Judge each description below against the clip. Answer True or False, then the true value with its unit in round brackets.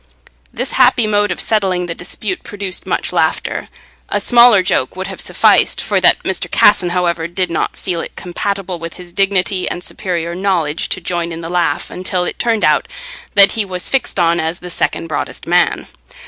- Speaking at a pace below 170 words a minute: False (185 wpm)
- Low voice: False (180 Hz)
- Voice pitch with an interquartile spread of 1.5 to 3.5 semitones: True (2.5 semitones)